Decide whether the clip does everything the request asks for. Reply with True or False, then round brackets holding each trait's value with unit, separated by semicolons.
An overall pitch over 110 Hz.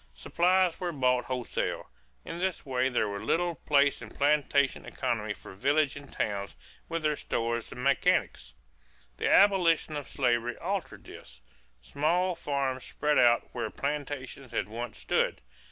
True (140 Hz)